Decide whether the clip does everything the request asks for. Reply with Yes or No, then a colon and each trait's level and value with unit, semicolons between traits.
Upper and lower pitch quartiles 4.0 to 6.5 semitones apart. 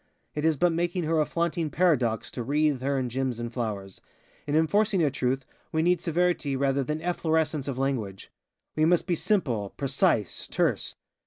Yes: average, 4.6 semitones